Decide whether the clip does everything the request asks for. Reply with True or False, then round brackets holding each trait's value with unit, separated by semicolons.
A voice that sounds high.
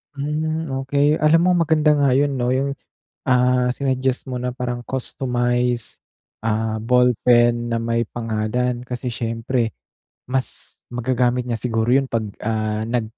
False (125 Hz)